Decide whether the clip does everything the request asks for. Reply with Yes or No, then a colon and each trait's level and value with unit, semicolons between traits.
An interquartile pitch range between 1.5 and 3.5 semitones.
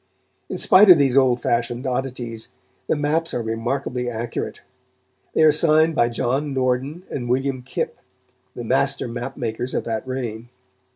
Yes: average, 2.7 semitones